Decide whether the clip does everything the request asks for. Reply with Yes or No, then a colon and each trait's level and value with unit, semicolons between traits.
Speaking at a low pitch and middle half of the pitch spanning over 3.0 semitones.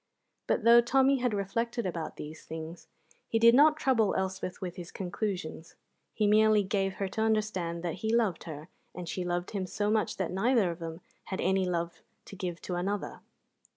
No: high, 195 Hz; average, 3.8 semitones